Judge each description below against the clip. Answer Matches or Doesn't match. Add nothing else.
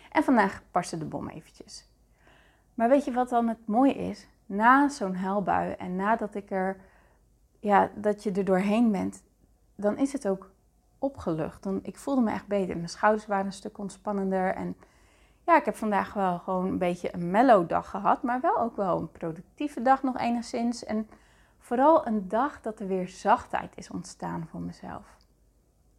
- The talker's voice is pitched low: Doesn't match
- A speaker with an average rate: Matches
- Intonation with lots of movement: Doesn't match